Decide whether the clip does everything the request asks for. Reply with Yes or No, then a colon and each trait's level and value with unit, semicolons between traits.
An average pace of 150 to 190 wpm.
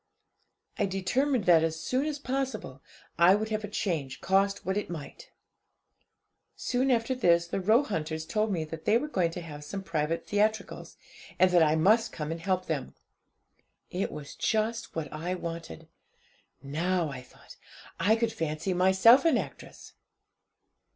Yes: average, 155 wpm